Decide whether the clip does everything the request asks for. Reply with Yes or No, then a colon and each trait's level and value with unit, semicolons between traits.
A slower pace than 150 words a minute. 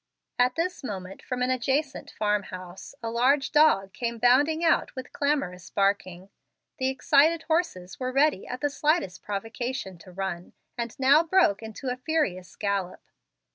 No: average, 155 wpm